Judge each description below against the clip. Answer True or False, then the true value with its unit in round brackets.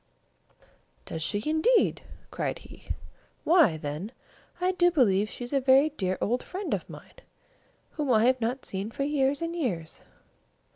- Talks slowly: False (155 wpm)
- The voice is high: True (260 Hz)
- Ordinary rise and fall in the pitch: False (7.3 semitones)